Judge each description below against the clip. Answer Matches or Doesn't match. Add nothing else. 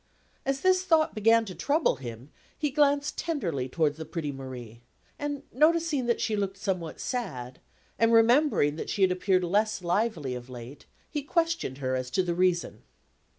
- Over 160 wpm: Matches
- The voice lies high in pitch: Matches